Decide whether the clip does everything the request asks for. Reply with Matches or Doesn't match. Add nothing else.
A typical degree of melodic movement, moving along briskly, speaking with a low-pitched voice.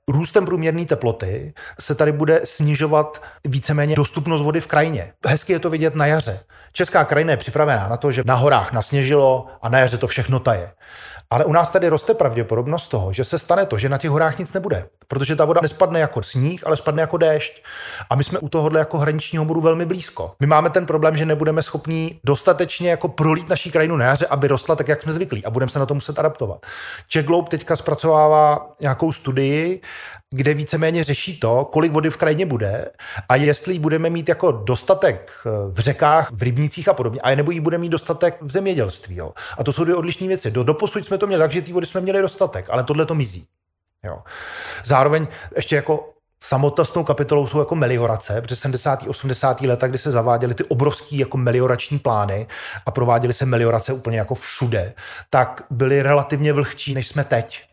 Doesn't match